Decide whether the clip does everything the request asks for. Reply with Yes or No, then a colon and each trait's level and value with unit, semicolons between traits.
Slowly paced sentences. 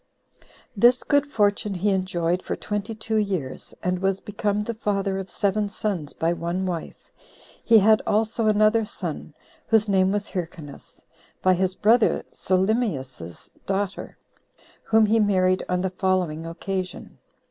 No: average, 145 wpm